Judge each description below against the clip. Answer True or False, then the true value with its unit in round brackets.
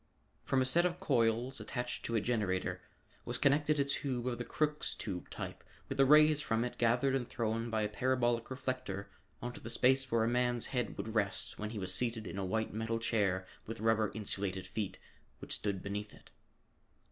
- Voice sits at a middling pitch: False (115 Hz)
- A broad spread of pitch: False (3.3 semitones)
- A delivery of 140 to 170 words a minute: False (195 wpm)